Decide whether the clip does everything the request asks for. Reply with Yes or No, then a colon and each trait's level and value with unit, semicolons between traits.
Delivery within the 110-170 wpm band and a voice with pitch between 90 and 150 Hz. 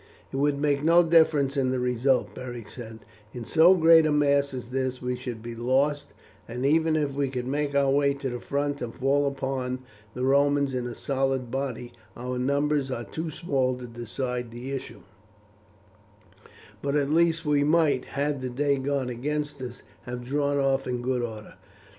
No: average, 185 wpm; low, 135 Hz